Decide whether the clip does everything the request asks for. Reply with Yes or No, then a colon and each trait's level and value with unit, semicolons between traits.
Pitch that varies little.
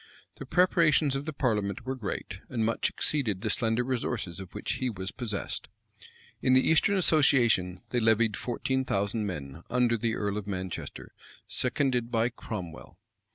No: average, 4.4 semitones